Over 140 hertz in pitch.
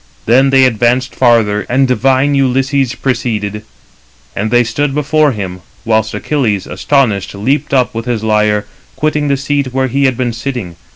No: low, 125 Hz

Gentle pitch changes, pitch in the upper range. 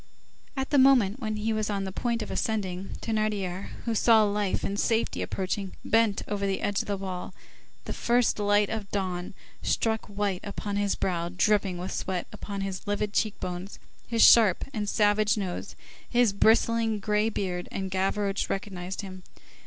Yes: narrow, 2.2 semitones; high, 205 Hz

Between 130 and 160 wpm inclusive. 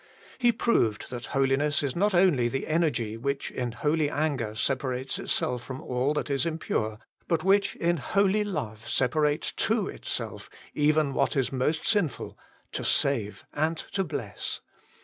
Yes: average, 150 wpm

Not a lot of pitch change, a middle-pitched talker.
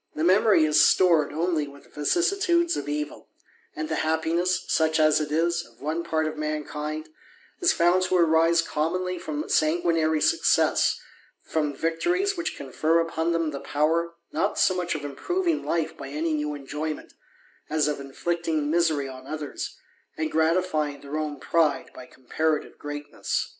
Yes: narrow, 2.3 semitones; medium, 160 Hz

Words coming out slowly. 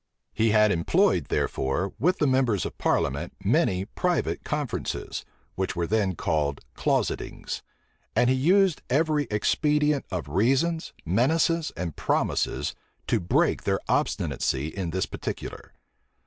Yes: slow, 125 wpm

